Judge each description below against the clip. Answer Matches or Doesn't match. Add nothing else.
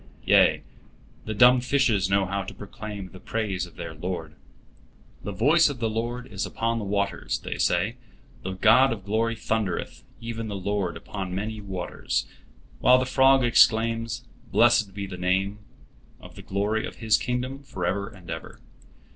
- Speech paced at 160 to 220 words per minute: Matches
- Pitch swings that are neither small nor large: Matches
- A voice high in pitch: Doesn't match